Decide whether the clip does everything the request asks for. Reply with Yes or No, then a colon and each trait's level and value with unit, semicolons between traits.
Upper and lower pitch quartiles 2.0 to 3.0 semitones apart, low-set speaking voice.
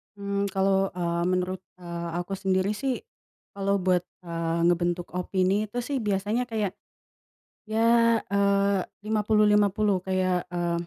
No: narrow, 2.4 semitones; high, 195 Hz